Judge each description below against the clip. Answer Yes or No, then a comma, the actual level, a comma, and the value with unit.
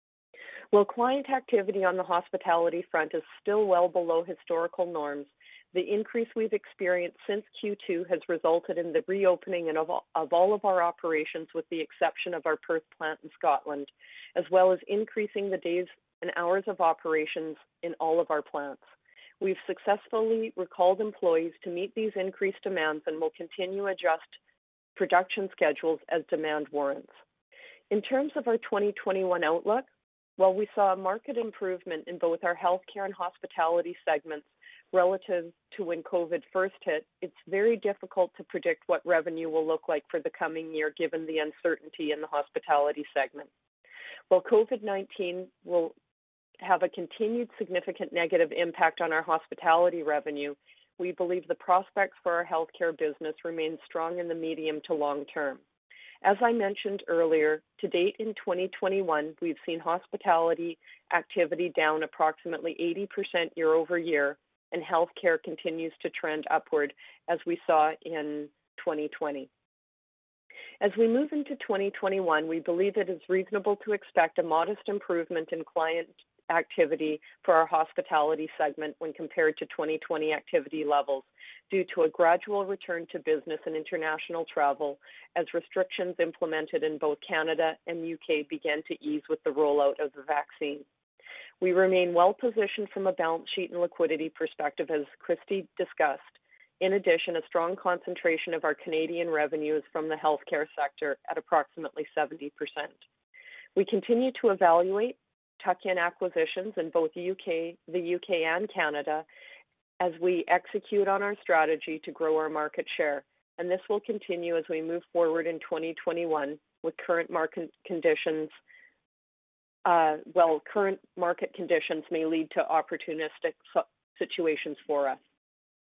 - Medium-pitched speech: Yes, medium, 170 Hz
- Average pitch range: Yes, average, 3.5 semitones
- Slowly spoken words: No, average, 150 wpm